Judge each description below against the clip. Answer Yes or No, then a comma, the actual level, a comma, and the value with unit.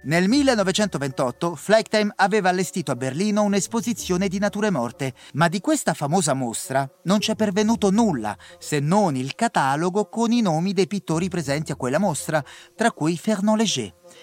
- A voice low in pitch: No, high, 195 Hz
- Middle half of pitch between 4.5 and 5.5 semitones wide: Yes, average, 5.2 semitones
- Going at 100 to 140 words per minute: No, average, 155 wpm